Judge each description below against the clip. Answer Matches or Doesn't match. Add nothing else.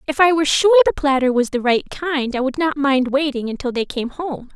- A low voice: Doesn't match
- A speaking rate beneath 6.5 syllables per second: Matches